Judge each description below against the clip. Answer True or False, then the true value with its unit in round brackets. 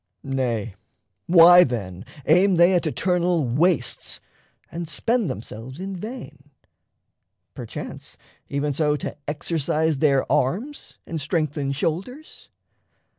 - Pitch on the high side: False (155 Hz)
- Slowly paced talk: True (105 wpm)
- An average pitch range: True (4.6 semitones)